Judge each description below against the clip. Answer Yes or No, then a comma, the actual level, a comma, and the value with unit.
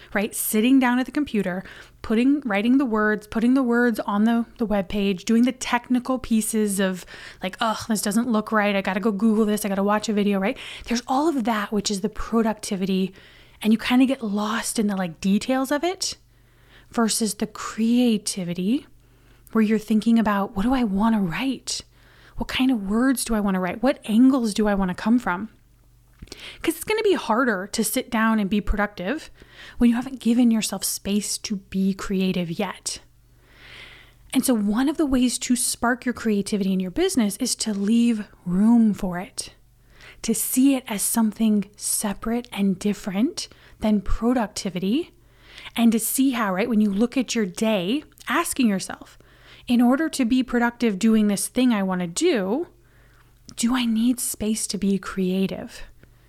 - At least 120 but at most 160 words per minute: No, average, 185 wpm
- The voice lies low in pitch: No, high, 220 Hz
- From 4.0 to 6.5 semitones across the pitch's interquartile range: No, average, 3.3 semitones